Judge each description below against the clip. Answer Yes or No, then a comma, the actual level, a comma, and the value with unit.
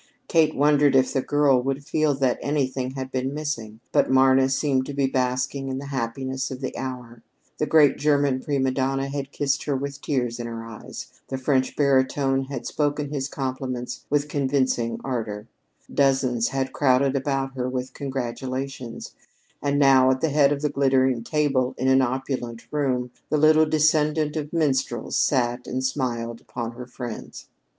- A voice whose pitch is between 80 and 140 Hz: Yes, low, 135 Hz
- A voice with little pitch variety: Yes, narrow, 1.9 semitones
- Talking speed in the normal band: Yes, average, 170 wpm